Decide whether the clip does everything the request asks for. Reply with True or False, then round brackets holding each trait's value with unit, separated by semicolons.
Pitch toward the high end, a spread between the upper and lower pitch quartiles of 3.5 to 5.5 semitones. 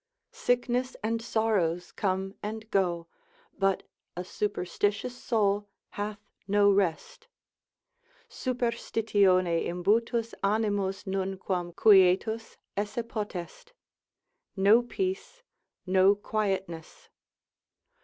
False (205 Hz; 2.9 semitones)